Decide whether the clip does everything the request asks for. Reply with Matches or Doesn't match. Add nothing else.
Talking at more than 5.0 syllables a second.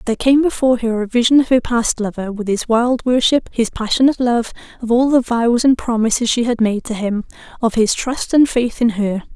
Matches